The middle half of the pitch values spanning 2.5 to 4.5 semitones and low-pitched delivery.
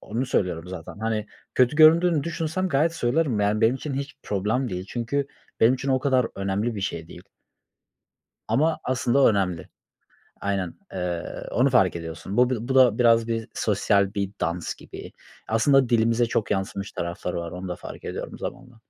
No: average, 5.2 semitones; low, 115 Hz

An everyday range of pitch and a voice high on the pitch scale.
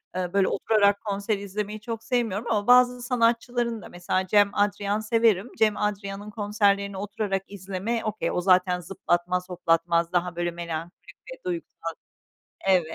Yes: average, 3.2 semitones; high, 200 Hz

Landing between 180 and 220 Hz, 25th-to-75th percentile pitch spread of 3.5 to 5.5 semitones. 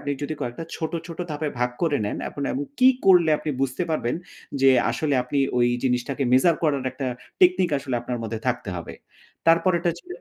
No: medium, 145 Hz; average, 5.0 semitones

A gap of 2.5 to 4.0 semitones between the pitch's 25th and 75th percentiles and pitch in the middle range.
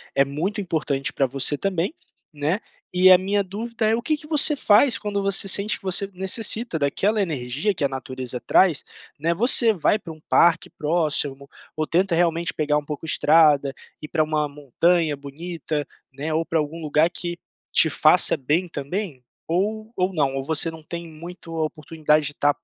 No: average, 4.6 semitones; medium, 165 Hz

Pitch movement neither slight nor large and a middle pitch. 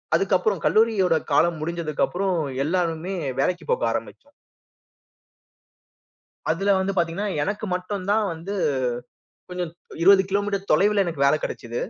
Yes: average, 3.2 semitones; medium, 180 Hz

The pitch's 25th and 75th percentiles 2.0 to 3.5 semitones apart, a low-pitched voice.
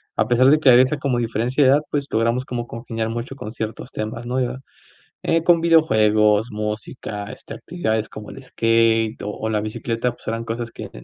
Yes: average, 2.8 semitones; low, 115 Hz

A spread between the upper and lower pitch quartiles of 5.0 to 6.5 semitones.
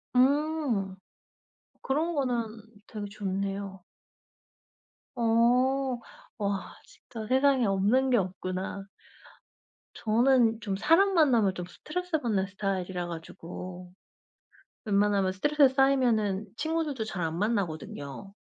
Yes: wide, 5.5 semitones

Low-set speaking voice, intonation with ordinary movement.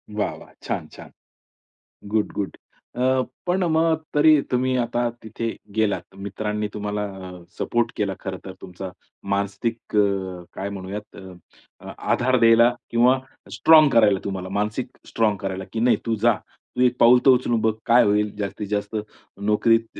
Yes: low, 110 Hz; average, 3.1 semitones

